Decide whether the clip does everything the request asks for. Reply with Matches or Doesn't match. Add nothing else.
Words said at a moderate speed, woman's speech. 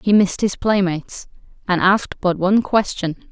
Matches